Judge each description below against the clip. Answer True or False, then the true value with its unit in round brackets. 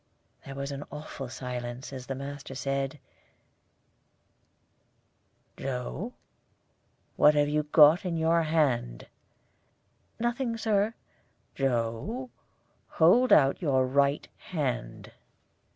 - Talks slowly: True (90 wpm)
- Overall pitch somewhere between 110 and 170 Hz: True (140 Hz)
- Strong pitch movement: False (4.1 semitones)